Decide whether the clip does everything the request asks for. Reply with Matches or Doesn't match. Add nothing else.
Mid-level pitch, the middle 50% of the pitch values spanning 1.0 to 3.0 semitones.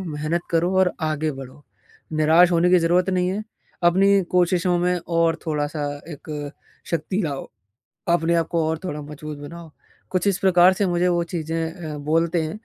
Matches